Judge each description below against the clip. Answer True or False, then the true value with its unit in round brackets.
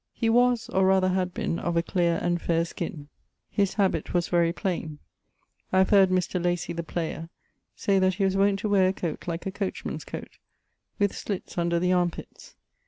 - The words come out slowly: False (205 wpm)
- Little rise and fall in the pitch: True (2.1 semitones)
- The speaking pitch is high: False (180 Hz)